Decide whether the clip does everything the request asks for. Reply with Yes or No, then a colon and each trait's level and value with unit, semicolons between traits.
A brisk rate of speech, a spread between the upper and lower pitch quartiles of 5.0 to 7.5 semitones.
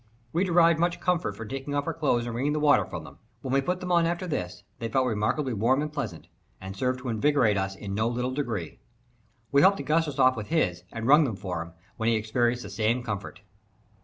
Yes: fast, 230 wpm; wide, 5.6 semitones